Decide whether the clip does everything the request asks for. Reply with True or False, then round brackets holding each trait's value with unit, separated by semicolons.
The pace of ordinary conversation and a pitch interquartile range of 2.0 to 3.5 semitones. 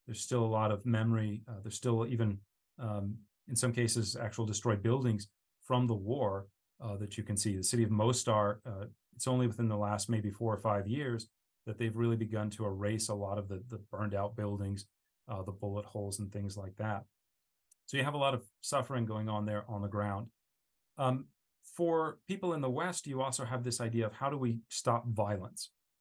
False (210 wpm; 2.7 semitones)